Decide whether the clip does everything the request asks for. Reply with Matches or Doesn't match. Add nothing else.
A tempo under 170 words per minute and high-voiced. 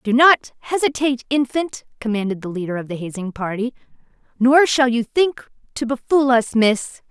Matches